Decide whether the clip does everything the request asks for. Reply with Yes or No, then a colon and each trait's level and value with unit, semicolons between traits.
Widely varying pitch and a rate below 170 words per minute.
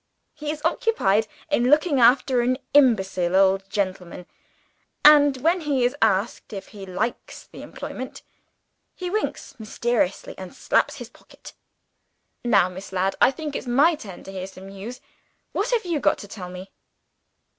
Yes: wide, 7.1 semitones; average, 155 wpm